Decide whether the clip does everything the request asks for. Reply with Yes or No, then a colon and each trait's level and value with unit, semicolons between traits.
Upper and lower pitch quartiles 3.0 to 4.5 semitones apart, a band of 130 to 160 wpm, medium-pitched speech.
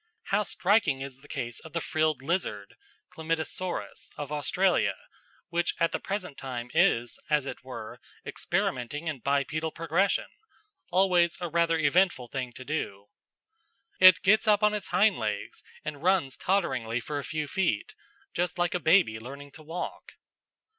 No: average, 5.1 semitones; average, 155 wpm; medium, 155 Hz